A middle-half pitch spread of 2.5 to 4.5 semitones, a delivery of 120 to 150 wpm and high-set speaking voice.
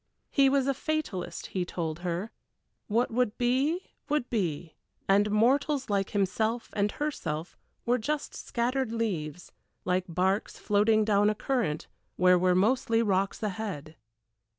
No: average, 5.2 semitones; slow, 135 wpm; high, 210 Hz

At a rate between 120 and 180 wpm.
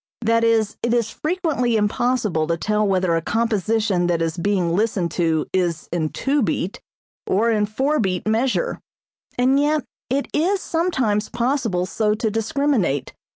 Yes: average, 155 wpm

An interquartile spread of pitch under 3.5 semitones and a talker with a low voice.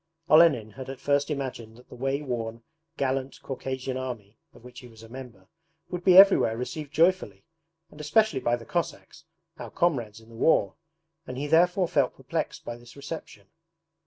No: average, 4.4 semitones; low, 130 Hz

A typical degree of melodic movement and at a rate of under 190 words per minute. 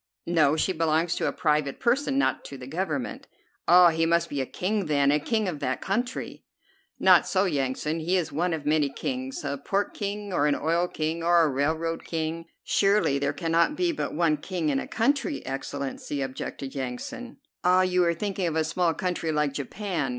No: average, 4.2 semitones; average, 195 wpm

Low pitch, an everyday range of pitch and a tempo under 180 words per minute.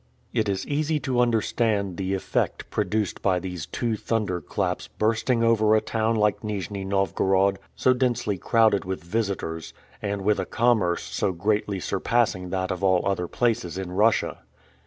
Yes: low, 100 Hz; average, 3.2 semitones; average, 155 wpm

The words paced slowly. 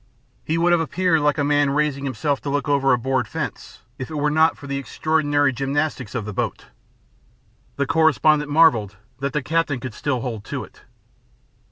No: average, 190 wpm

